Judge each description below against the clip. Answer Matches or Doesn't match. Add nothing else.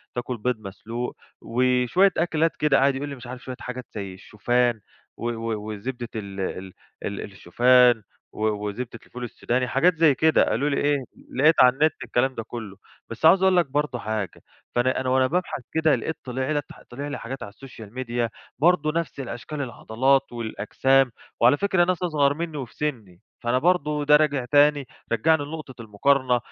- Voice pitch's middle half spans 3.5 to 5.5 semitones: Matches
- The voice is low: Matches